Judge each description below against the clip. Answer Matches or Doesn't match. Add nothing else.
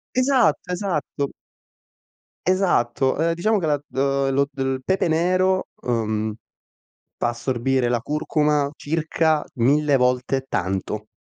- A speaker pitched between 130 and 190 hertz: Matches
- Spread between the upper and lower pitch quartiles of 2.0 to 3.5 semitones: Doesn't match